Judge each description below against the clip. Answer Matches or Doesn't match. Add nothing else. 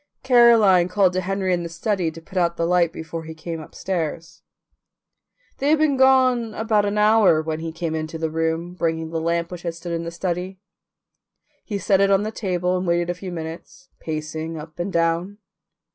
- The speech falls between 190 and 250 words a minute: Matches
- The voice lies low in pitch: Doesn't match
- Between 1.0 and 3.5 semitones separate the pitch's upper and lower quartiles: Matches